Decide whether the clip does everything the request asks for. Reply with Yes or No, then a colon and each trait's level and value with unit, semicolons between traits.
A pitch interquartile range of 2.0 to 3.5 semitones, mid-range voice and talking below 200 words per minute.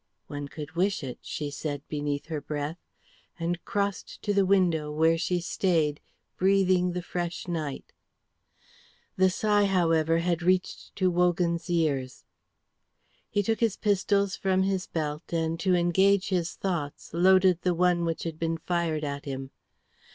Yes: average, 3.0 semitones; medium, 175 Hz; average, 150 wpm